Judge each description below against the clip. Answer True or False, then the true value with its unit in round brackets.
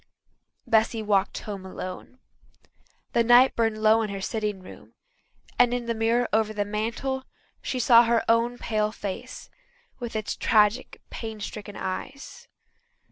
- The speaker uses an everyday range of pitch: False (2.2 semitones)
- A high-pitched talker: True (225 Hz)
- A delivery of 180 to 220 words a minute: False (140 wpm)